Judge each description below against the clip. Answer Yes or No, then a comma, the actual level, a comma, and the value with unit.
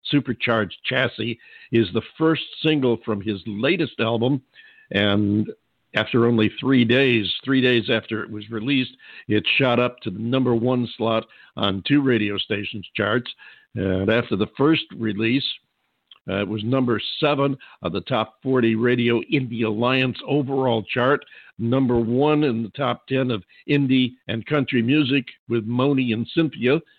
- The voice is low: Yes, low, 120 Hz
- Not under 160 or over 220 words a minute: No, average, 150 wpm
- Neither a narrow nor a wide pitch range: Yes, average, 3.2 semitones